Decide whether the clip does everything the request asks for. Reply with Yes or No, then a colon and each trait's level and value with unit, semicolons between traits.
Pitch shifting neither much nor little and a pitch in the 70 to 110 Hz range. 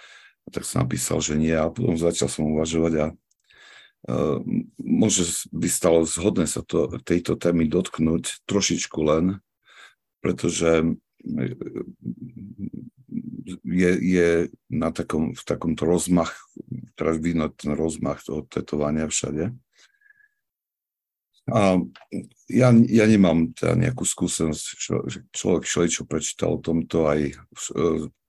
Yes: average, 4.4 semitones; very low, 85 Hz